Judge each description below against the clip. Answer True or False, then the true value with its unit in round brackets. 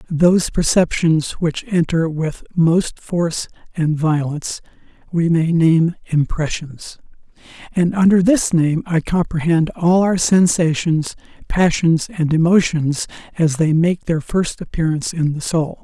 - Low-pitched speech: False (165 Hz)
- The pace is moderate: False (130 wpm)